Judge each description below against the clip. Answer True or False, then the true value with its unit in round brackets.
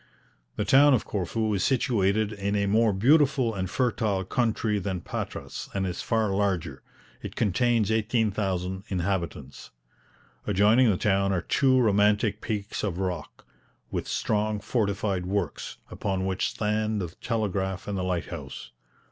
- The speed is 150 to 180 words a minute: False (140 wpm)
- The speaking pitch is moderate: False (100 Hz)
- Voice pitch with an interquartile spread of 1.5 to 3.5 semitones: True (2.7 semitones)